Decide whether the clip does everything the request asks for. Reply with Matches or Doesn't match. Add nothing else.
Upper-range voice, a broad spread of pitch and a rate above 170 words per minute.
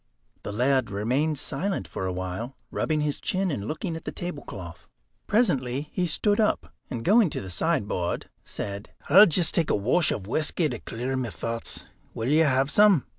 Doesn't match